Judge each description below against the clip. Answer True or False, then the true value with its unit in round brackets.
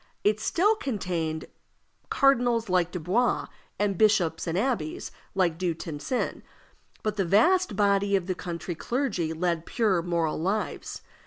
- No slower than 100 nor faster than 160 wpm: True (135 wpm)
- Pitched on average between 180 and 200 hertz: True (190 Hz)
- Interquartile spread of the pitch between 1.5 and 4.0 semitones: False (4.7 semitones)